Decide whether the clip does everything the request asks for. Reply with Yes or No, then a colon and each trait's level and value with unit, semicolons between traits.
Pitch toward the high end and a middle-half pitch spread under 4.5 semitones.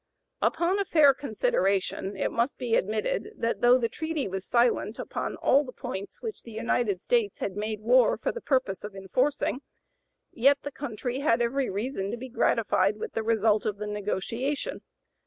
No: high, 240 Hz; average, 5.1 semitones